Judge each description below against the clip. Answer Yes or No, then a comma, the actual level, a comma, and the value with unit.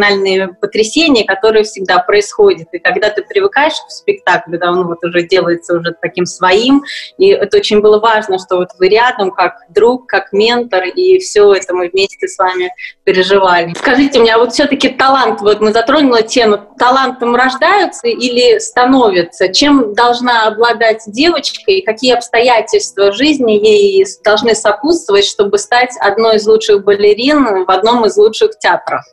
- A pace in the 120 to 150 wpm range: No, fast, 160 wpm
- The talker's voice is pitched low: No, high, 230 Hz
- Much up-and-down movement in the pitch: Yes, wide, 7.0 semitones